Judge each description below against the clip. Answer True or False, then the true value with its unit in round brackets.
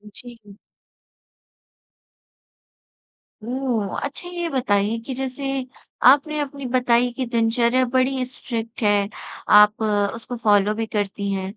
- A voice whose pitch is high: True (240 Hz)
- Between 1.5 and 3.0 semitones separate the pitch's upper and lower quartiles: False (3.8 semitones)